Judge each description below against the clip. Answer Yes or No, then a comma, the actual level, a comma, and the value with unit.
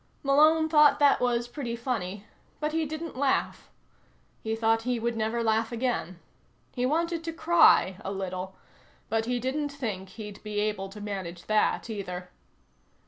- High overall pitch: Yes, high, 230 Hz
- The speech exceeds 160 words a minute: No, average, 155 wpm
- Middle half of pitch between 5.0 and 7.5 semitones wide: Yes, wide, 5.5 semitones